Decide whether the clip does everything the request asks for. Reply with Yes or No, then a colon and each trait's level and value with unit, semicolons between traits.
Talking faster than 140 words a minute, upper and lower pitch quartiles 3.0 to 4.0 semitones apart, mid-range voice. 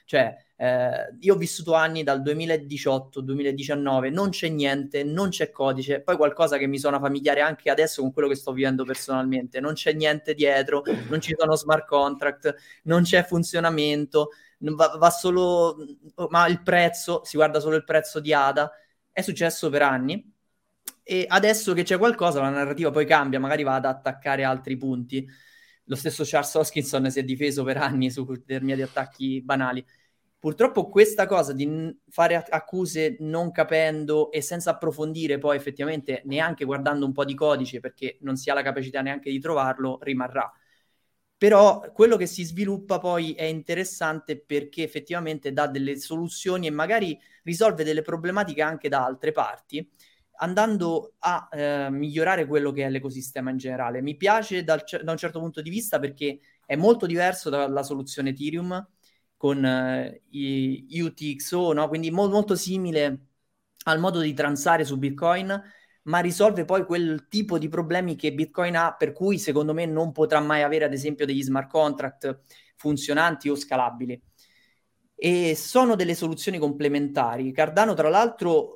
Yes: average, 165 wpm; average, 3.6 semitones; medium, 155 Hz